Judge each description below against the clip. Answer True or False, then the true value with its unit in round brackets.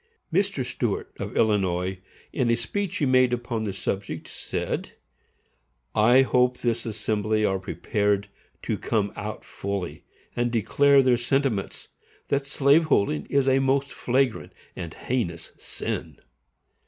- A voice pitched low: True (120 Hz)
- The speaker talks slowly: True (130 wpm)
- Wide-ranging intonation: False (4.7 semitones)